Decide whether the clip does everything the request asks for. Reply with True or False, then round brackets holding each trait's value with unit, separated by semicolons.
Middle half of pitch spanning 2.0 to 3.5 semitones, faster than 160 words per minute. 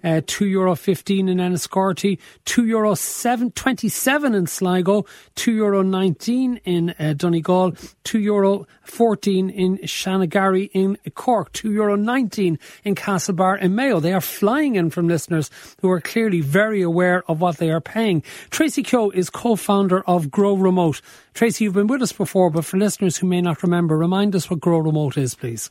True (3.0 semitones; 175 wpm)